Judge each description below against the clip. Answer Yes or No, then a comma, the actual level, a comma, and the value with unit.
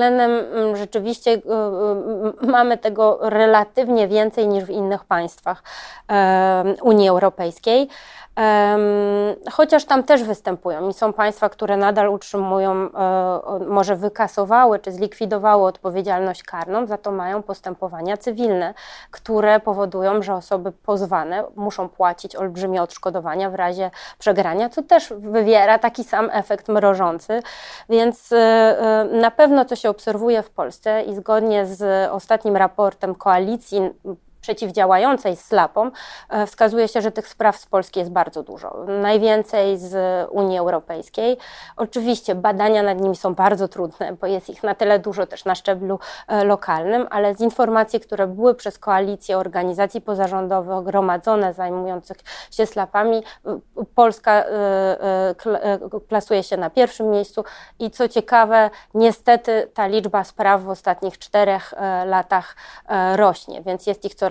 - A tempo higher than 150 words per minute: No, average, 125 wpm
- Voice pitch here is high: Yes, high, 205 Hz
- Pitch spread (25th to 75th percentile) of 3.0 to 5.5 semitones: No, narrow, 2.5 semitones